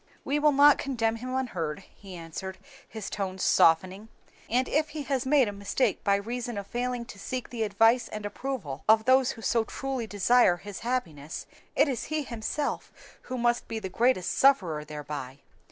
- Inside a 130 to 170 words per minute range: No, average, 180 wpm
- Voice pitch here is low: No, high, 225 Hz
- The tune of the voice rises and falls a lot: No, average, 5.0 semitones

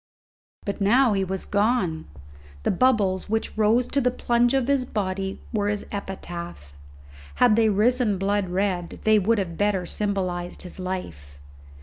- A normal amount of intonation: Yes, average, 3.4 semitones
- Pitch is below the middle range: No, high, 200 Hz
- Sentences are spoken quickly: No, average, 150 wpm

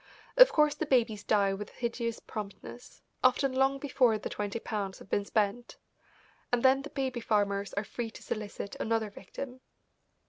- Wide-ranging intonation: No, average, 4.3 semitones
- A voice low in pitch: No, high, 230 Hz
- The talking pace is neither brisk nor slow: Yes, average, 165 wpm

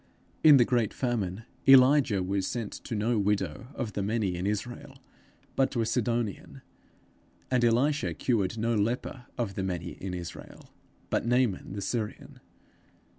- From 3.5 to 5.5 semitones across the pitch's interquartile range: Yes, average, 3.8 semitones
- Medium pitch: No, low, 115 Hz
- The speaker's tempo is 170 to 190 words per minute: No, average, 150 wpm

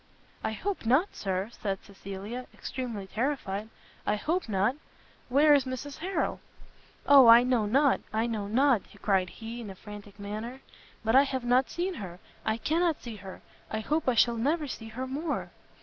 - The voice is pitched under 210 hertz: No, high, 235 Hz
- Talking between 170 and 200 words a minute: Yes, average, 175 wpm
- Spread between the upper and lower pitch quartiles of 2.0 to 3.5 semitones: No, average, 4.9 semitones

